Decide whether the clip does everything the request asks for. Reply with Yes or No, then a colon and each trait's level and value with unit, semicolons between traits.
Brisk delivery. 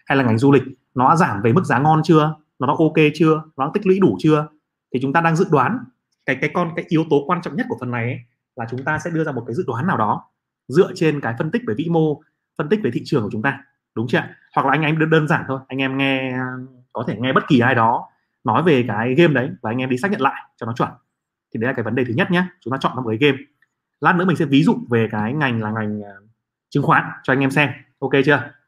Yes: fast, 290 wpm